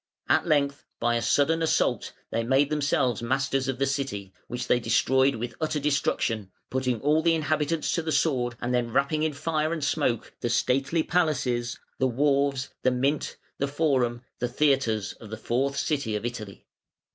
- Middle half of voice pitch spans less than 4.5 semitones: Yes, average, 3.5 semitones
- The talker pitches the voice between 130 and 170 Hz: Yes, low, 135 Hz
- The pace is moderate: Yes, average, 175 wpm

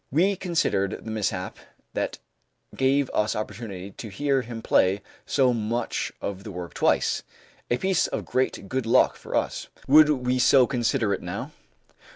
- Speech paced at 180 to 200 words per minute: No, average, 160 wpm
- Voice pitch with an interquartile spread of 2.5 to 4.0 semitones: No, average, 4.7 semitones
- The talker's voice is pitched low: Yes, low, 120 Hz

